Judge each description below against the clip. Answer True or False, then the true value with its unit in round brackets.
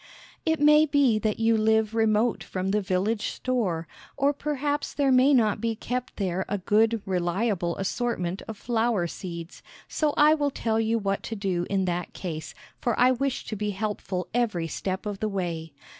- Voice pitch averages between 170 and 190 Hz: False (215 Hz)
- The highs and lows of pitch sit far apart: False (4.6 semitones)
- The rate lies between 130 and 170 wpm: False (180 wpm)